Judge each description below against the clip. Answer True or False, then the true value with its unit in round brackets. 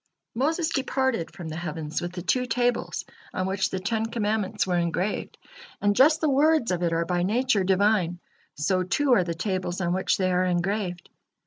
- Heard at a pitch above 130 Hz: True (190 Hz)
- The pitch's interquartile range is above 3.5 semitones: True (4.8 semitones)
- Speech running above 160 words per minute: True (190 wpm)